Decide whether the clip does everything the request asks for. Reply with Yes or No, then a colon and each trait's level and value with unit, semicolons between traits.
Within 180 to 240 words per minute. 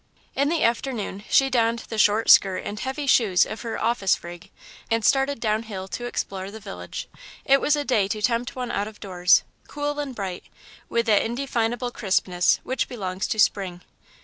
Yes: average, 185 wpm